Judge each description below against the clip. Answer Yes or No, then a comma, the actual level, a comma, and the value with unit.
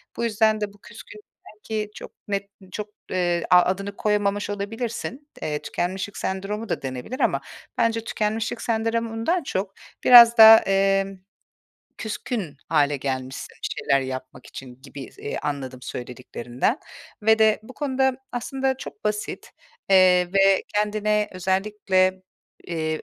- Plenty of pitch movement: No, average, 4.1 semitones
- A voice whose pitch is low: No, high, 200 Hz